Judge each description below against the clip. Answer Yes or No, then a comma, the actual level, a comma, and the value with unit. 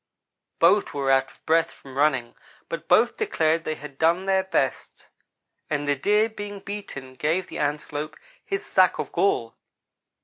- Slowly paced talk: No, average, 160 wpm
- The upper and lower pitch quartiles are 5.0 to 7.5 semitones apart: Yes, average, 5.3 semitones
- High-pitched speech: No, medium, 160 Hz